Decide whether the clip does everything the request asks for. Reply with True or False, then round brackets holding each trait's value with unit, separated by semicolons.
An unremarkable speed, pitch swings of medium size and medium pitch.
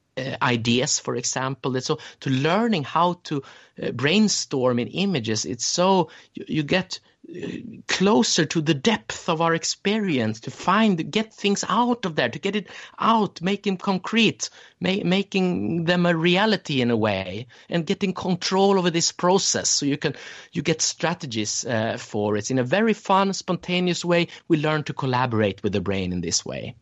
False (175 wpm; 7.0 semitones; 165 Hz)